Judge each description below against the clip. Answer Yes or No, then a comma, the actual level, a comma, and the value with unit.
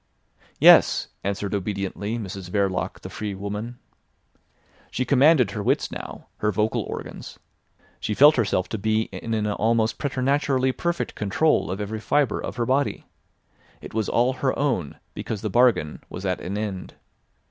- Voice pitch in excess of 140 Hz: No, low, 110 Hz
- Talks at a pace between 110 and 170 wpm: Yes, average, 155 wpm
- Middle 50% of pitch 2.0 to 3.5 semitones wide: No, average, 4.3 semitones